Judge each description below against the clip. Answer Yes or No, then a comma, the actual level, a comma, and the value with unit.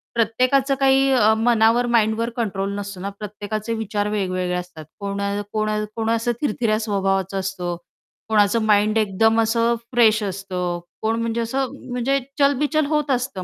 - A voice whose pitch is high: Yes, high, 220 Hz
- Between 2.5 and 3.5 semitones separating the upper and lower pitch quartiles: Yes, average, 3.1 semitones